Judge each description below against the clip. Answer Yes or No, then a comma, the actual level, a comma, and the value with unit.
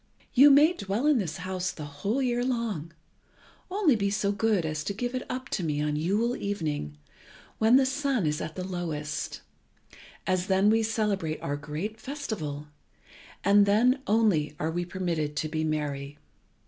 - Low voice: No, high, 190 Hz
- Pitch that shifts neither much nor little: No, wide, 6.9 semitones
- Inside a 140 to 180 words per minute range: Yes, average, 170 wpm